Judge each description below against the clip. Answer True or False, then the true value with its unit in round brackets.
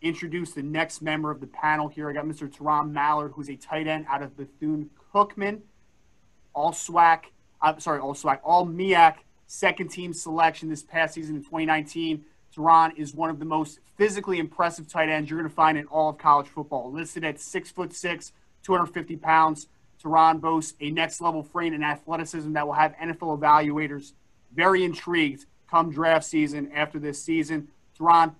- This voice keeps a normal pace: True (180 wpm)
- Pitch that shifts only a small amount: True (1.8 semitones)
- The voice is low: False (160 Hz)